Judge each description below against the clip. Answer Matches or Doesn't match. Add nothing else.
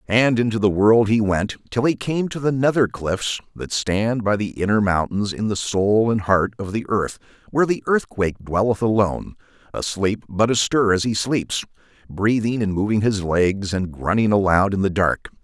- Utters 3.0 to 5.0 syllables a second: Matches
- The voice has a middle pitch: Doesn't match